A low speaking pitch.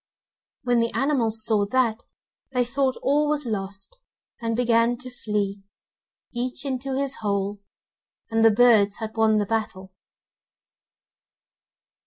No: high, 230 Hz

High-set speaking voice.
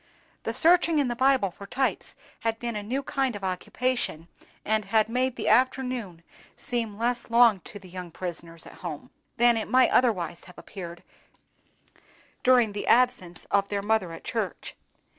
Yes: high, 220 Hz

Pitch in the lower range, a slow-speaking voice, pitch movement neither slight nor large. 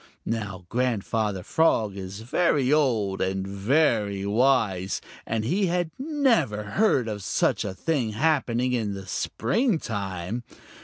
No: low, 115 Hz; slow, 120 wpm; wide, 6.3 semitones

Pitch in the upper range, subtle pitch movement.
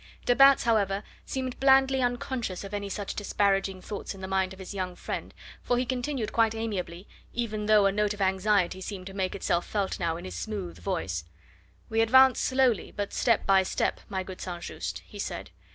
No: high, 205 Hz; average, 3.6 semitones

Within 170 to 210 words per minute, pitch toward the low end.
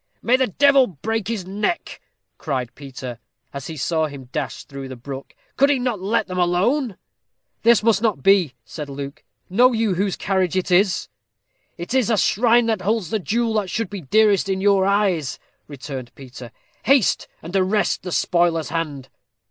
No: average, 175 wpm; high, 190 Hz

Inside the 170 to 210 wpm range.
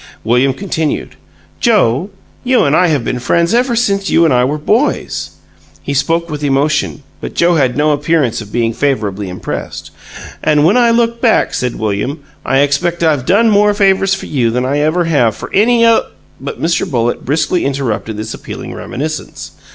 Yes: average, 180 wpm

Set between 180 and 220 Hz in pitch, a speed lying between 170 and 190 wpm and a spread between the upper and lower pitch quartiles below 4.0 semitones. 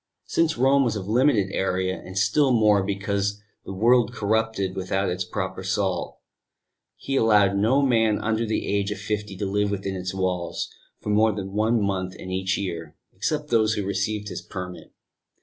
No: low, 100 Hz; average, 175 wpm; narrow, 2.6 semitones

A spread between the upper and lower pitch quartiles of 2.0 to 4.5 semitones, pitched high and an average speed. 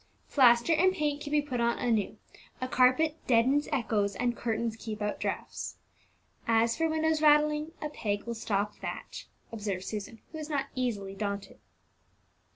No: wide, 5.5 semitones; high, 240 Hz; average, 160 wpm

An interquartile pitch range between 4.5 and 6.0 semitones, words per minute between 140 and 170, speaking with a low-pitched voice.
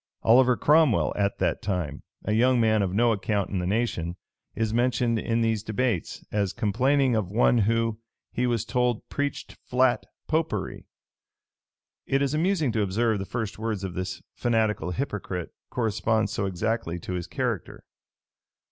No: average, 3.7 semitones; average, 155 wpm; low, 110 Hz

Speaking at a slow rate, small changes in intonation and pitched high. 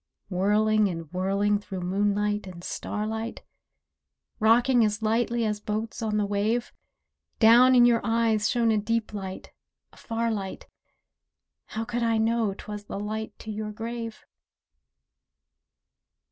Yes: slow, 130 wpm; narrow, 1.9 semitones; high, 215 Hz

